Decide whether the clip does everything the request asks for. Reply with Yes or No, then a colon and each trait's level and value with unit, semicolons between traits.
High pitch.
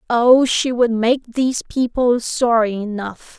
Yes: high, 235 Hz